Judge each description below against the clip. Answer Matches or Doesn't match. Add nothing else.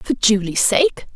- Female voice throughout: Matches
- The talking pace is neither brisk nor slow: Matches